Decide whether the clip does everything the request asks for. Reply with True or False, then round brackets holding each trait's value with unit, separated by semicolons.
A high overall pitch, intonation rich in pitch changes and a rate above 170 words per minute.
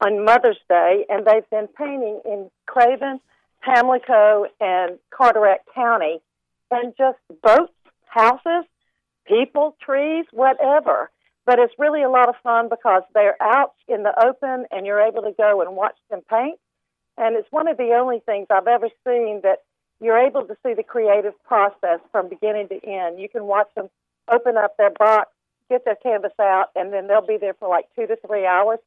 False (225 Hz; 3.5 semitones; 180 wpm)